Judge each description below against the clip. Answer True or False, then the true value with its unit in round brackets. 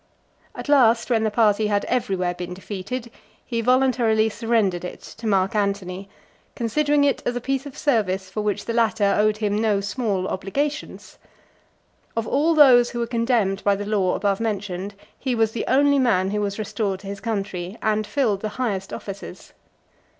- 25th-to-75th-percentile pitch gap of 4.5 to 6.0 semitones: False (3.4 semitones)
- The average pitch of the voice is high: True (215 Hz)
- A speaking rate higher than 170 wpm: True (180 wpm)